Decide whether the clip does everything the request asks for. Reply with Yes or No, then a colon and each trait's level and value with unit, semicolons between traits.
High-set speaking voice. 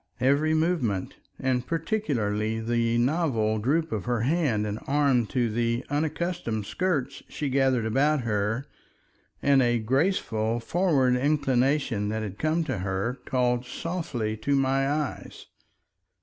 No: low, 130 Hz